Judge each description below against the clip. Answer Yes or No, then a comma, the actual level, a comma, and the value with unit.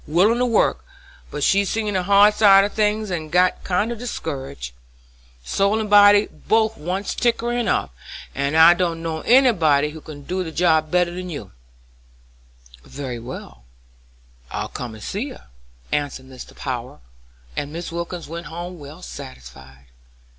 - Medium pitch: Yes, medium, 170 Hz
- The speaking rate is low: No, average, 160 wpm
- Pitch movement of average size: No, wide, 6.1 semitones